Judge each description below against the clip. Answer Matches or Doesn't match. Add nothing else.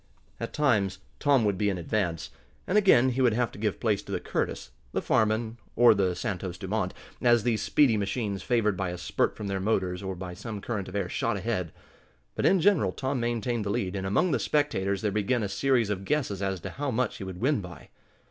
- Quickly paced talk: Matches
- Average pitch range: Matches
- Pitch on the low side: Matches